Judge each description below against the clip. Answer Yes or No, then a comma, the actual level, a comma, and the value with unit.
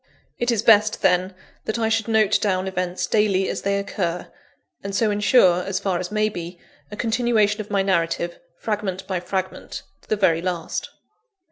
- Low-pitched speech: No, high, 200 Hz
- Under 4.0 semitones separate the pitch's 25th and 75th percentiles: Yes, average, 2.7 semitones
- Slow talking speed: No, average, 175 wpm